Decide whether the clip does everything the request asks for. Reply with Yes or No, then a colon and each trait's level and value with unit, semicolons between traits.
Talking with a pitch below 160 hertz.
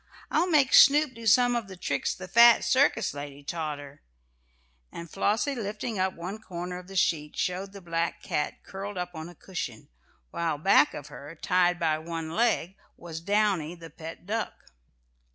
No: medium, 180 Hz